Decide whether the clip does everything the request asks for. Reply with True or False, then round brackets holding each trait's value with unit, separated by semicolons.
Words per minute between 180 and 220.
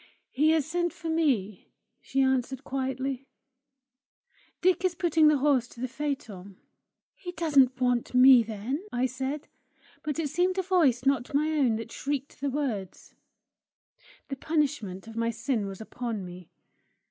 False (150 wpm)